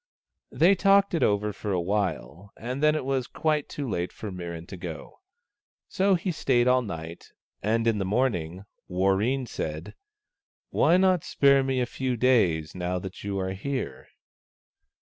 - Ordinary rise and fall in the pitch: No, wide, 6.8 semitones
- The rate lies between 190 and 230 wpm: No, average, 165 wpm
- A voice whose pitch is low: Yes, low, 110 Hz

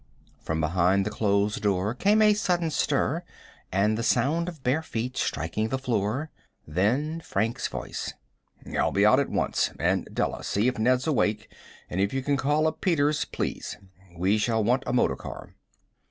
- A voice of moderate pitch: No, low, 120 Hz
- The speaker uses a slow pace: No, average, 170 wpm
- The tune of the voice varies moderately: No, wide, 6.5 semitones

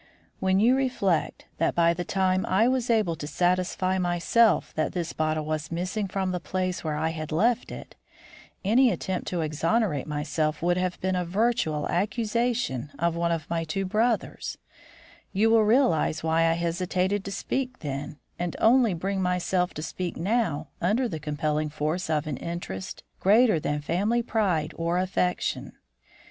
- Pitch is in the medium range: Yes, medium, 180 Hz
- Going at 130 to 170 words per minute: Yes, average, 165 wpm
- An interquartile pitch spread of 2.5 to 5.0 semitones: Yes, average, 4.4 semitones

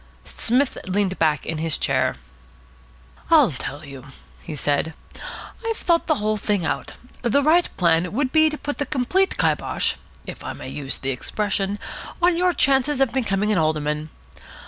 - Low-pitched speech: No, high, 210 Hz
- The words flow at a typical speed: Yes, average, 165 wpm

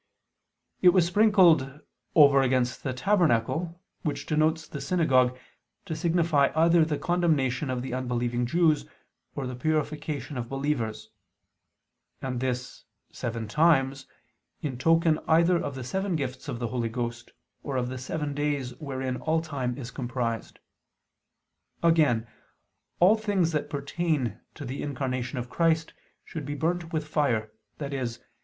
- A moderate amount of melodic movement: Yes, average, 4.4 semitones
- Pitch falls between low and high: Yes, medium, 145 Hz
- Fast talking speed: No, average, 140 wpm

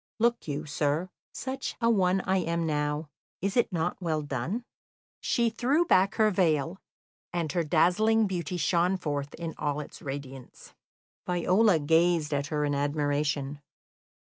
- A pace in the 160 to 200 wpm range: No, average, 145 wpm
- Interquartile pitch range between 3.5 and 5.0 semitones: Yes, average, 4.4 semitones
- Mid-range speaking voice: Yes, medium, 165 Hz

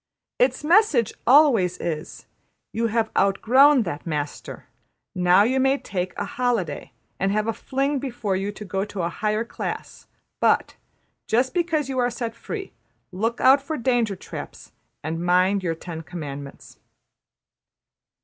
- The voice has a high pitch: Yes, high, 220 Hz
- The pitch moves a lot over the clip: Yes, wide, 6.2 semitones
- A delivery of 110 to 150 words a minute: Yes, average, 145 wpm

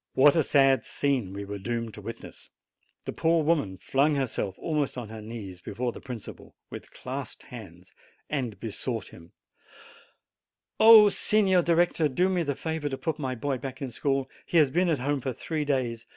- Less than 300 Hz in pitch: Yes, low, 135 Hz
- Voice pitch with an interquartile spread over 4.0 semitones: Yes, average, 5.0 semitones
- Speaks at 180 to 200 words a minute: Yes, average, 185 wpm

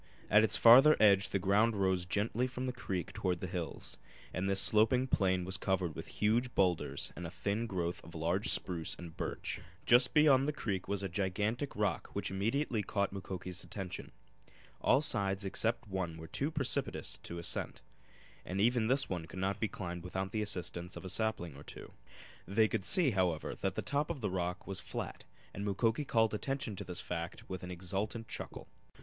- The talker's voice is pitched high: No, low, 100 Hz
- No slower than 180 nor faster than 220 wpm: Yes, average, 190 wpm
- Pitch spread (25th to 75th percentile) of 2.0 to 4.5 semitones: Yes, average, 3.8 semitones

